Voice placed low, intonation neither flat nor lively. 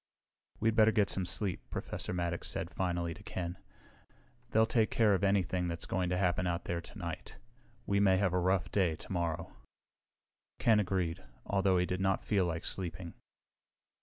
No: very low, 90 Hz; narrow, 2.3 semitones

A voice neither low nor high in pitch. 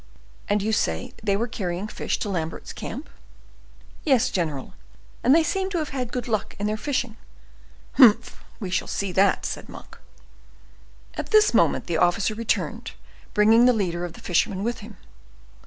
No: high, 215 Hz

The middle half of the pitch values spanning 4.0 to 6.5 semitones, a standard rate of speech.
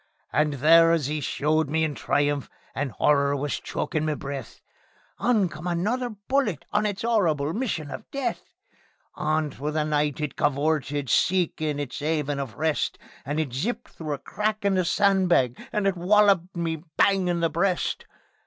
Yes: average, 4.8 semitones; average, 170 wpm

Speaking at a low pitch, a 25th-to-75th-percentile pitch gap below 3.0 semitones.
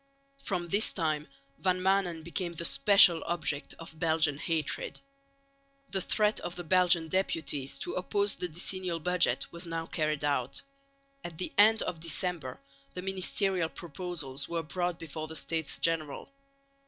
No: medium, 170 Hz; narrow, 2.5 semitones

